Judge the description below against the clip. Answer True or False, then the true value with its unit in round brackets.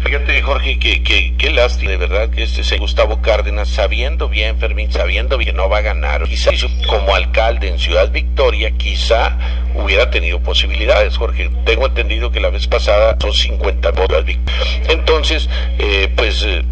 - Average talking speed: True (170 wpm)